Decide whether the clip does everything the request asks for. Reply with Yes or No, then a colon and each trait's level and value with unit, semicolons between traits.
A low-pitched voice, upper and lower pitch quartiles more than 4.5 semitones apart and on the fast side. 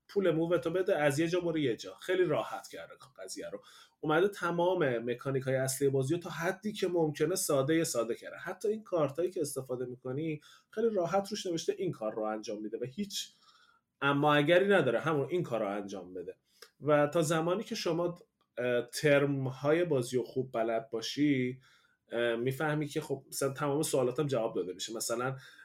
No: medium, 150 Hz; average, 5.2 semitones; fast, 185 wpm